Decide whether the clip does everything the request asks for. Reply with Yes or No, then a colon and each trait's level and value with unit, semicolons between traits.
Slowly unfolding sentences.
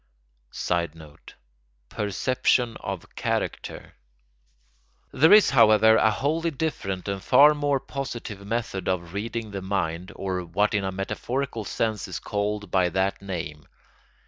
Yes: slow, 125 wpm